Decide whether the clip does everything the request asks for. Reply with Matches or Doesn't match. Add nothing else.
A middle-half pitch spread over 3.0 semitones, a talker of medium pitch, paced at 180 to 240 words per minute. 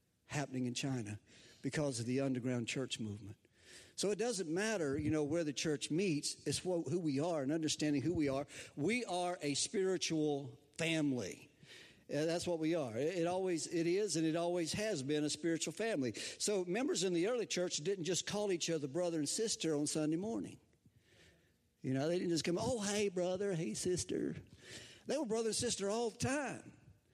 Matches